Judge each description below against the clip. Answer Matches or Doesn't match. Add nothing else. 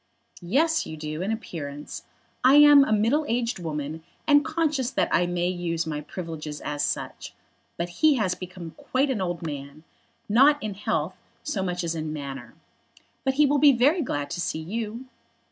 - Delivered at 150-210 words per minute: Matches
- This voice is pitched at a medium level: Matches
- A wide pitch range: Matches